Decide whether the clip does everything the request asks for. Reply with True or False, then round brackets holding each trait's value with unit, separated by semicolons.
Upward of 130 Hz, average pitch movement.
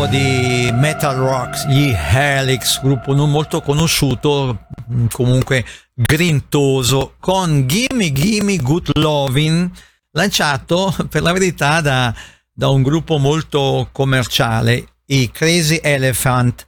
True (140 Hz; 3.5 semitones)